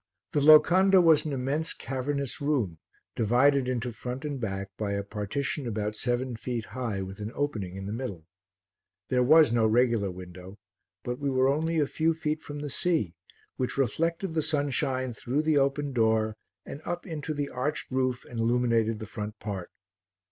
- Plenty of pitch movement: No, average, 5.0 semitones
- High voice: No, low, 130 Hz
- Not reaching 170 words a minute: No, average, 175 wpm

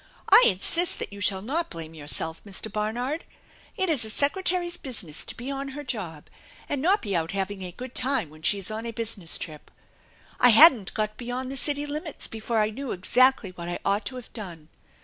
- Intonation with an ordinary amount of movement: No, wide, 6.3 semitones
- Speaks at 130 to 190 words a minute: No, fast, 205 wpm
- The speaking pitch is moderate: No, high, 225 Hz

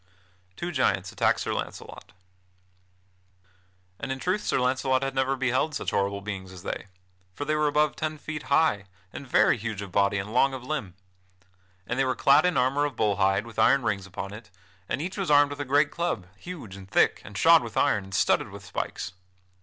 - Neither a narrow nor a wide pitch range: No, wide, 6.5 semitones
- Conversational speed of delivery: No, fast, 210 wpm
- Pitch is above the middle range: No, low, 130 Hz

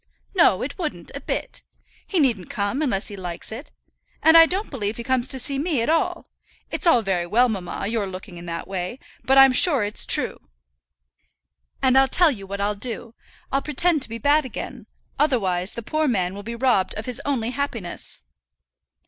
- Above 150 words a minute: Yes, average, 195 wpm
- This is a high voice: Yes, high, 235 Hz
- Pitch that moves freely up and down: Yes, wide, 6.0 semitones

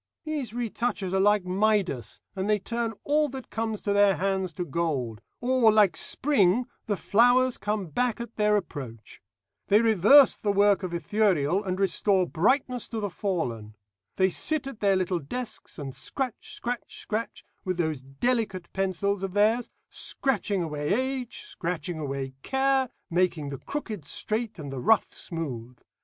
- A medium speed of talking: Yes, average, 155 wpm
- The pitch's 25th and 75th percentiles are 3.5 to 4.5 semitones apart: No, average, 5.2 semitones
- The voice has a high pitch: Yes, high, 200 Hz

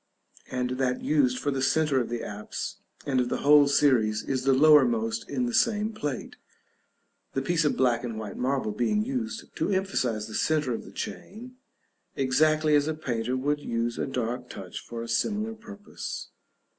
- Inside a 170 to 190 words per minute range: Yes, average, 180 wpm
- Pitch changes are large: Yes, wide, 7.3 semitones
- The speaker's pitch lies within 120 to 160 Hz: Yes, medium, 140 Hz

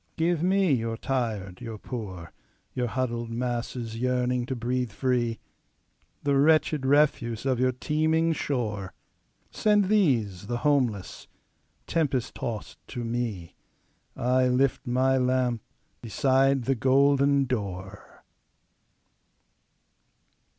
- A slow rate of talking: Yes, slow, 95 wpm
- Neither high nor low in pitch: No, low, 125 Hz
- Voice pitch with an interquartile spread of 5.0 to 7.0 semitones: No, average, 3.1 semitones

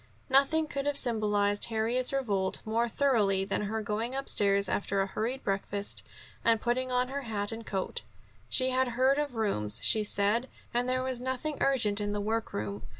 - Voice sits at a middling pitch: No, high, 225 Hz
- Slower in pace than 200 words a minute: Yes, average, 180 wpm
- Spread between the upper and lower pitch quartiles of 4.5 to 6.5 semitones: No, average, 4.0 semitones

